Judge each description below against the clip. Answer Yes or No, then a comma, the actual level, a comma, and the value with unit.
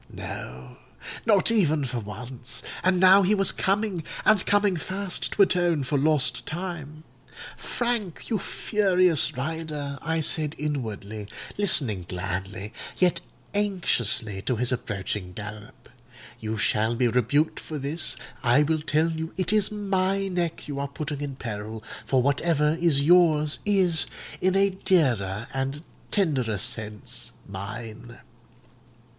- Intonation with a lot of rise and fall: Yes, wide, 7.5 semitones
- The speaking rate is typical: No, slow, 125 wpm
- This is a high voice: No, medium, 150 Hz